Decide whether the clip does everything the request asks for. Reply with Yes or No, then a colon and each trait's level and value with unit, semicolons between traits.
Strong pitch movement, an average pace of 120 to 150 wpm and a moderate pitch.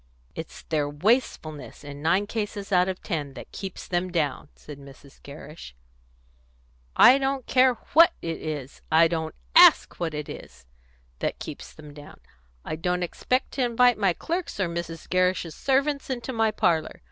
No: wide, 7.0 semitones; average, 160 wpm; medium, 175 Hz